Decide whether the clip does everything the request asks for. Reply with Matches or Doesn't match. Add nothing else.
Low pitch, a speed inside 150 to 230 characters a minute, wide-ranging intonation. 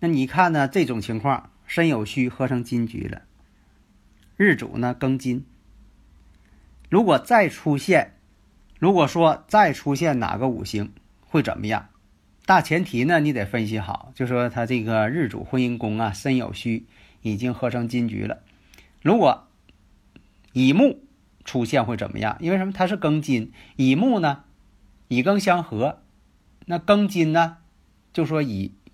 Matches